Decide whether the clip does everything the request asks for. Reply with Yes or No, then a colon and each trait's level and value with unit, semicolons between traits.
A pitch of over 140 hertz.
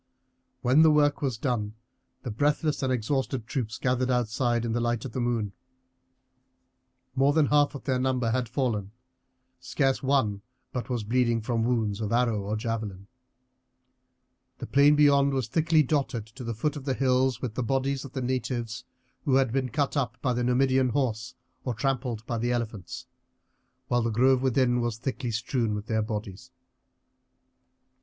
No: low, 125 Hz